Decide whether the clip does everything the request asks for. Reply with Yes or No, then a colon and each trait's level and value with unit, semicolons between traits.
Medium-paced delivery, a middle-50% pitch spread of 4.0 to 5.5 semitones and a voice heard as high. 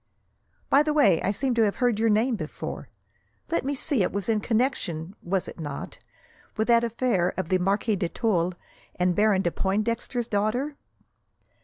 Yes: average, 175 wpm; average, 4.5 semitones; high, 215 Hz